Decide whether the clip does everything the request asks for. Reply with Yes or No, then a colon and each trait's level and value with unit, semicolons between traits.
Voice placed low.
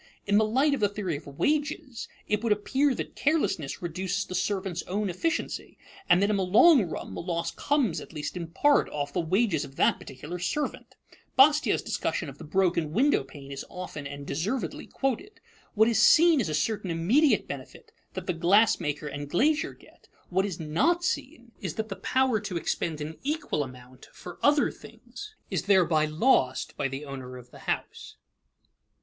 No: high, 190 Hz